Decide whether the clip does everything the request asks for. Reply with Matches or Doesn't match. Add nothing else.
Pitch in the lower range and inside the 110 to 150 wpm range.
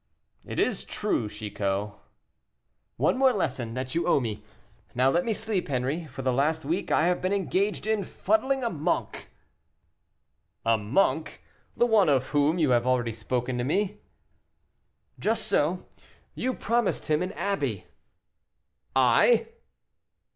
Doesn't match